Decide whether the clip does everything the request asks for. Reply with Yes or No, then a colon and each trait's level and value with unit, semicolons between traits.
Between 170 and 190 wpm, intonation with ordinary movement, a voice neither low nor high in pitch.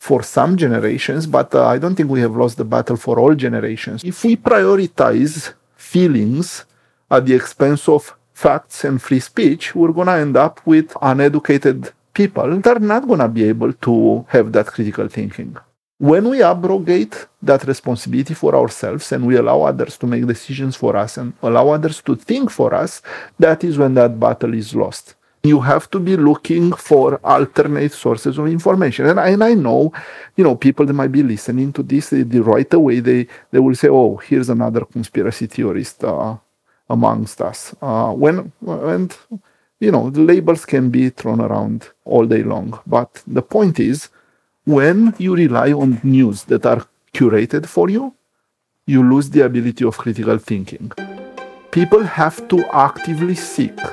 No: average, 175 wpm; wide, 5.8 semitones; medium, 145 Hz